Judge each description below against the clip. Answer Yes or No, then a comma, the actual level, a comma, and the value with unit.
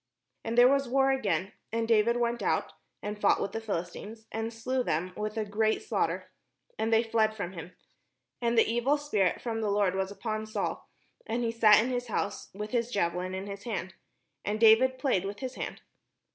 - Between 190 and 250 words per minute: Yes, average, 200 wpm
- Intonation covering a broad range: No, average, 2.7 semitones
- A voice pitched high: Yes, high, 220 Hz